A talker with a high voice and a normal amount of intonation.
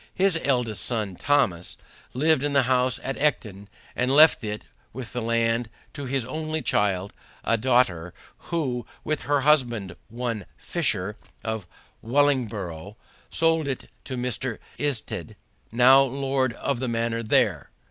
No: low, 125 Hz; average, 3.9 semitones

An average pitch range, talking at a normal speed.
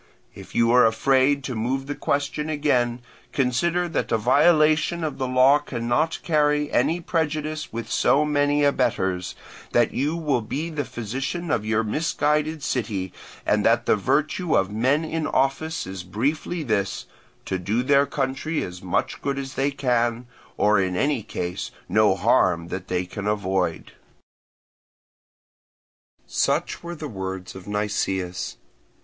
No: wide, 6.0 semitones; average, 145 wpm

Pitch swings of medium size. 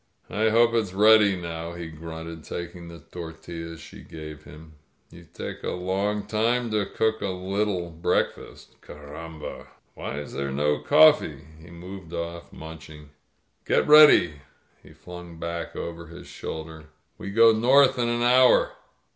Yes: average, 4.8 semitones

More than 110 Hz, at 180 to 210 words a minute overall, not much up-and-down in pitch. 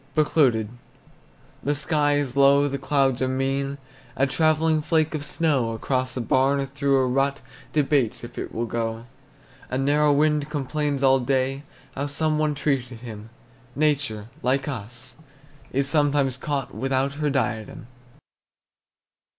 No: low, 135 Hz; average, 140 wpm; narrow, 2.2 semitones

